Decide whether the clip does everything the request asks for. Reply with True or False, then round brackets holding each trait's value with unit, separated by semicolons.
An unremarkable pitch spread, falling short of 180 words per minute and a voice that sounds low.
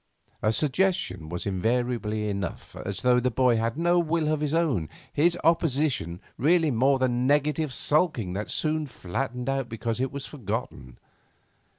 False (5.8 semitones; 155 wpm; 125 Hz)